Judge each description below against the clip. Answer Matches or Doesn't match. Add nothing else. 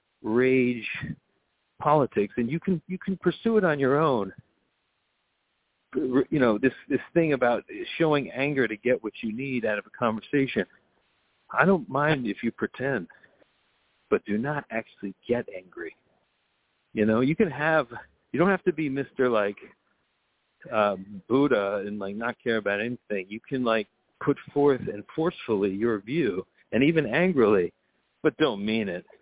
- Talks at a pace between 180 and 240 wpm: Doesn't match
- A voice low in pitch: Matches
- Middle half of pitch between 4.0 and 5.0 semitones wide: Doesn't match